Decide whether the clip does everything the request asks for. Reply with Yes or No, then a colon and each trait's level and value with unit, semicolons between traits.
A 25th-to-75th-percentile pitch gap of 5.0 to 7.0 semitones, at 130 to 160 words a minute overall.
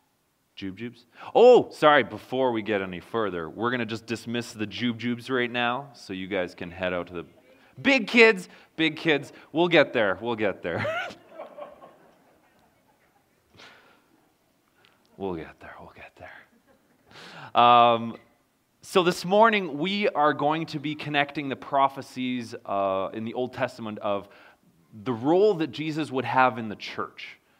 Yes: wide, 5.5 semitones; average, 150 wpm